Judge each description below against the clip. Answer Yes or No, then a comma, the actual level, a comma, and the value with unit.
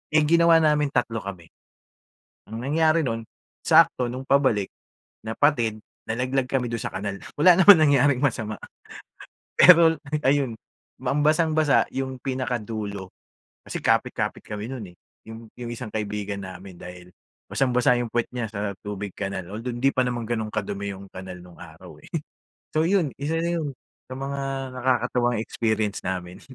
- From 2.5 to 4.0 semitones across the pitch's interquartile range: No, average, 5.3 semitones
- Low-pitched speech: Yes, low, 120 Hz